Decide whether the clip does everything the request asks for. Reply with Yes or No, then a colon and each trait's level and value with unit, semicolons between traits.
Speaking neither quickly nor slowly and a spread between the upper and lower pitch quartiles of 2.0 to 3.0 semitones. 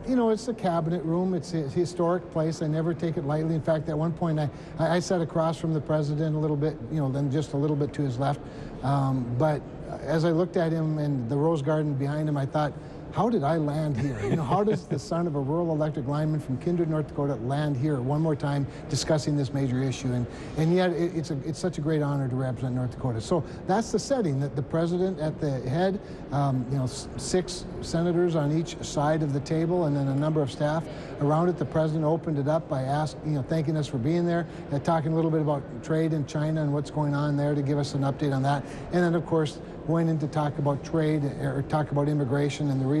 No: fast, 255 wpm; narrow, 2.5 semitones